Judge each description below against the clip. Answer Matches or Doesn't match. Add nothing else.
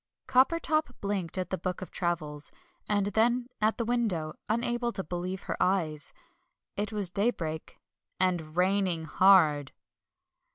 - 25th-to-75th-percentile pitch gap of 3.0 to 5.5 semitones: Matches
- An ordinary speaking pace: Doesn't match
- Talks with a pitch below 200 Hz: Matches